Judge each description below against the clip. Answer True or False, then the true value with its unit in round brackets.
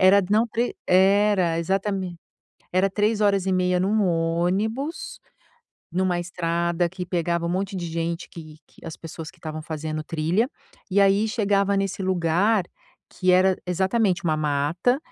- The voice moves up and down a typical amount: True (3.0 semitones)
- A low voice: False (185 Hz)